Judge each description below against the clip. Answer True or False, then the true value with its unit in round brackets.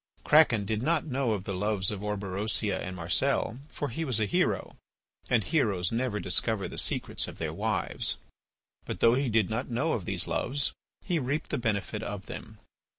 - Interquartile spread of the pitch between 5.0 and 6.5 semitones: False (4.5 semitones)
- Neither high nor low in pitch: False (110 Hz)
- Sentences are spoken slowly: False (185 wpm)